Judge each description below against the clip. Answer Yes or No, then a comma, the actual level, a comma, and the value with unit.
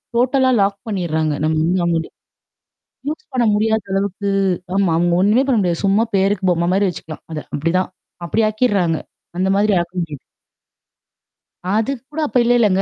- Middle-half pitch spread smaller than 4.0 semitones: No, average, 4.3 semitones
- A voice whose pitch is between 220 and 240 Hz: No, high, 195 Hz